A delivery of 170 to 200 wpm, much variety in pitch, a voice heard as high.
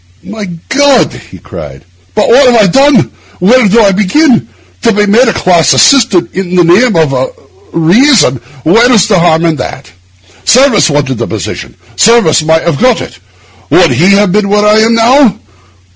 Yes: average, 175 wpm; wide, 6.0 semitones; high, 205 Hz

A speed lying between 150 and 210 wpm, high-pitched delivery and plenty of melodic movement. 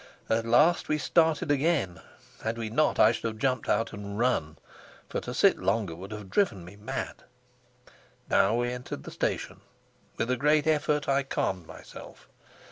No: average, 170 wpm; low, 115 Hz; wide, 6.2 semitones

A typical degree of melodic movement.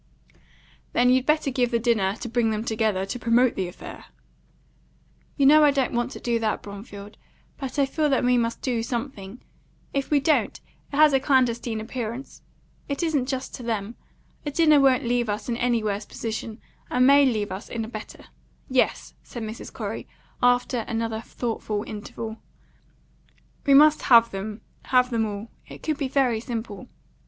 Yes: average, 3.3 semitones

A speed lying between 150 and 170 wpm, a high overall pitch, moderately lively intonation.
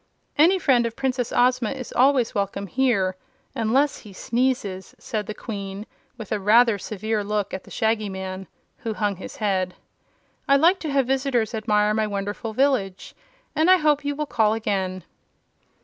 Yes: average, 165 wpm; high, 220 Hz; average, 4.7 semitones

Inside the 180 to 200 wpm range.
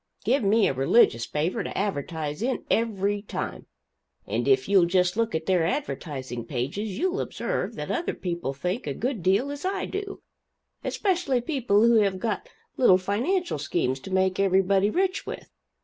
No: average, 165 wpm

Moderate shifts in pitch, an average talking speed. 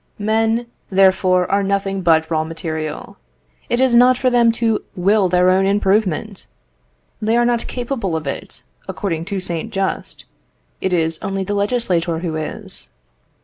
Yes: average, 4.4 semitones; average, 150 wpm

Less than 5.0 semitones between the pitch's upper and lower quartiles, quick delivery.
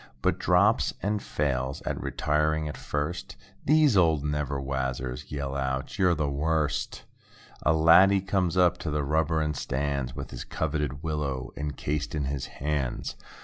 No: average, 2.7 semitones; average, 150 wpm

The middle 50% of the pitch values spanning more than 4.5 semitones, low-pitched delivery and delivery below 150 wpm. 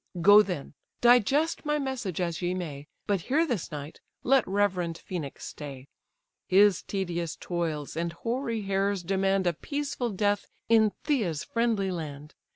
No: average, 5.3 semitones; high, 195 Hz; average, 140 wpm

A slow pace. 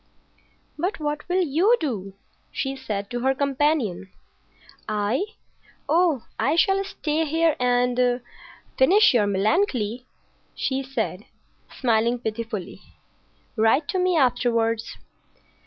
Yes: slow, 105 wpm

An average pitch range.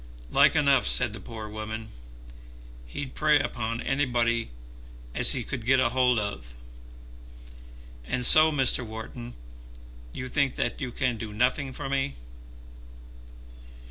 Yes: average, 3.3 semitones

